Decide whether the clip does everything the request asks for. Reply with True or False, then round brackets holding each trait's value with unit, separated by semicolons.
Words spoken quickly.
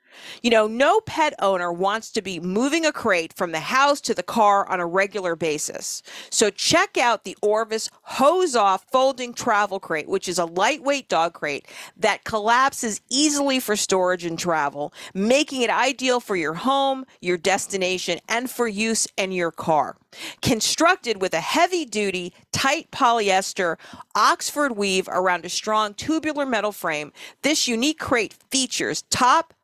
False (160 wpm)